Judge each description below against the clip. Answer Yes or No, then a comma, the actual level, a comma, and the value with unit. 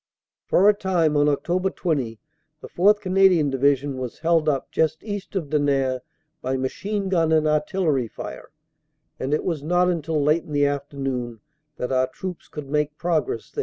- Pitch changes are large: No, average, 4.4 semitones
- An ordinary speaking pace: Yes, average, 170 wpm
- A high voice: No, medium, 150 Hz